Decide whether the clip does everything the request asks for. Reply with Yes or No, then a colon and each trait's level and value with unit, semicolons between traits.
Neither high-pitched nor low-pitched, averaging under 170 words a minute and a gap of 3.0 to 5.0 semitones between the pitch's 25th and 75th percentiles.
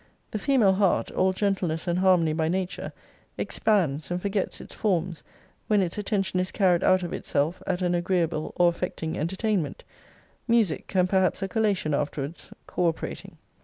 No: medium, 180 Hz; average, 160 wpm; narrow, 2.6 semitones